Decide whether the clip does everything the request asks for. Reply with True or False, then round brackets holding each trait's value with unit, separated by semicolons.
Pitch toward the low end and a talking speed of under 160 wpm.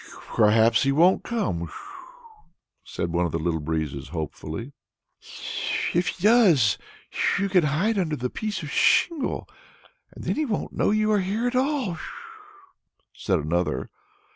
False (150 Hz; 145 wpm)